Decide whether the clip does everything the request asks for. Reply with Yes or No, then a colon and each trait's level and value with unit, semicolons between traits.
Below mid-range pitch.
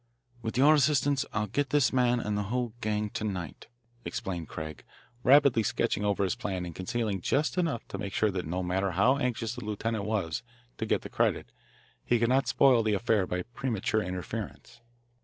Yes: low, 110 Hz